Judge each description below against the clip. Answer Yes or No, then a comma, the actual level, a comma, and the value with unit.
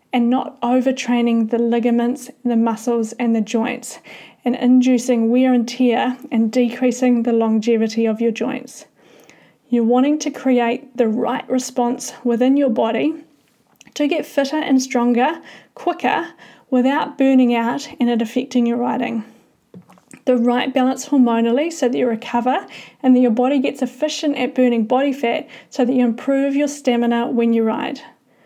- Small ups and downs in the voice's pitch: Yes, narrow, 1.8 semitones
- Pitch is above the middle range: Yes, high, 245 Hz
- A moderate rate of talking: Yes, average, 155 wpm